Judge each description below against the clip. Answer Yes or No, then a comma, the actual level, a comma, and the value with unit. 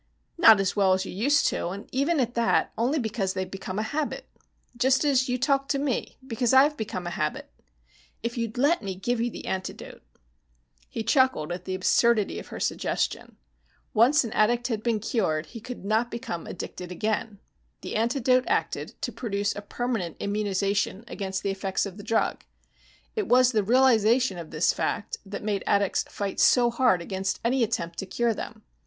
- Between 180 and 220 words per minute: Yes, average, 185 wpm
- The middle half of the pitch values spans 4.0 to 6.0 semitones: Yes, average, 4.3 semitones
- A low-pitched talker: No, high, 220 Hz